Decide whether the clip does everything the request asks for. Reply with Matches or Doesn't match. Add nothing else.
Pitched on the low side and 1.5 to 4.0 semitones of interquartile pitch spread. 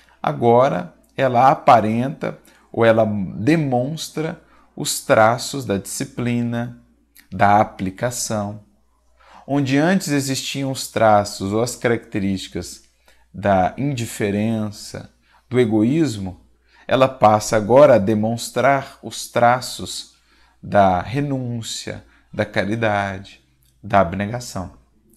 Matches